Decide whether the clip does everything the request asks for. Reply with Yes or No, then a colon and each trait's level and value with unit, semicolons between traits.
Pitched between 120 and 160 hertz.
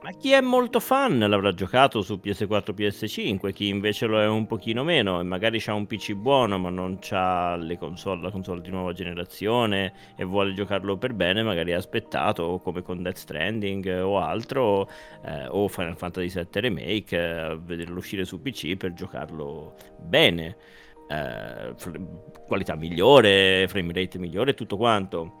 No: very low, 95 Hz